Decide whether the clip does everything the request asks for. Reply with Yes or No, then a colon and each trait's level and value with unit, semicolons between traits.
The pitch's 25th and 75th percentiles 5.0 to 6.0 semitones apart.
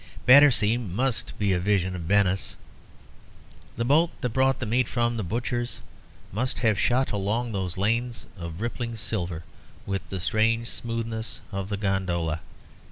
No: average, 3.7 semitones